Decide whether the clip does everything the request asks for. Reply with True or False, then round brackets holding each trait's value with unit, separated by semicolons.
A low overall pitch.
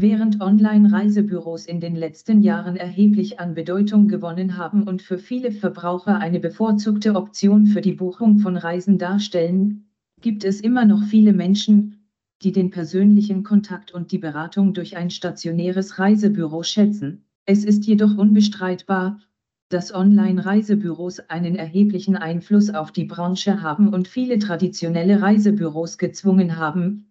False (195 Hz)